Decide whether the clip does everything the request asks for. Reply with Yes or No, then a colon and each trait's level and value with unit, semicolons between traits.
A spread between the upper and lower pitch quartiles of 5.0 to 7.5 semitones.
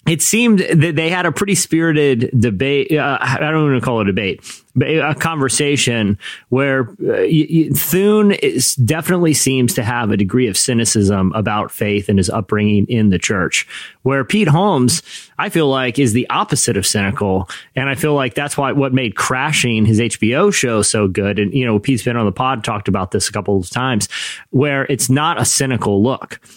Yes: wide, 5.6 semitones